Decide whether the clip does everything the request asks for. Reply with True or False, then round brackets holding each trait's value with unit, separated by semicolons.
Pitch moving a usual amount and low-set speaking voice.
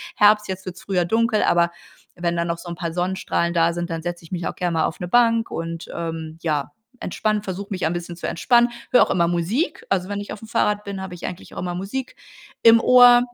False (3.6 semitones; 180 Hz)